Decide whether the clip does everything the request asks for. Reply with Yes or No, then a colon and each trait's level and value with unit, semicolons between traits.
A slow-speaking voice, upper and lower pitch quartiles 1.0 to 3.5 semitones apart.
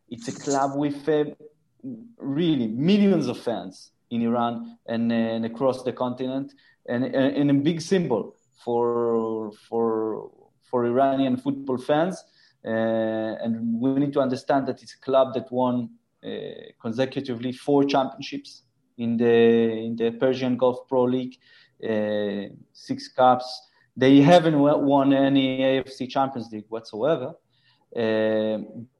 Yes: slow, 130 wpm; average, 3.2 semitones